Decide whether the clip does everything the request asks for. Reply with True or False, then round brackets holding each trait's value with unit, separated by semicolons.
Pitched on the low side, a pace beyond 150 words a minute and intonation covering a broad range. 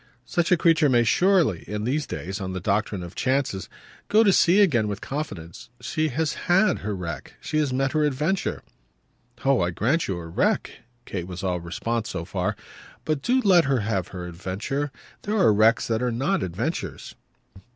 True (120 Hz; 190 wpm; 8.6 semitones)